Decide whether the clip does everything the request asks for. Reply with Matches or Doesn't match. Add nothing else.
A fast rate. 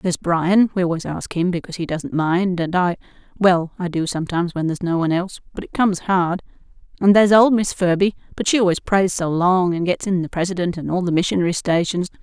Matches